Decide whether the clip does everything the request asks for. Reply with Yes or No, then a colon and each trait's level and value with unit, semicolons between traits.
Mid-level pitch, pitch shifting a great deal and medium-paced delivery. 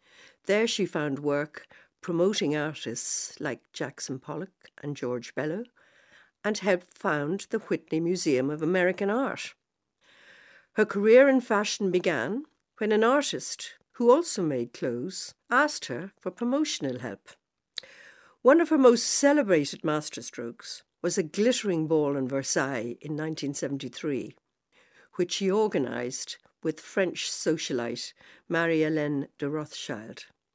No: medium, 180 Hz; wide, 7.2 semitones; slow, 120 wpm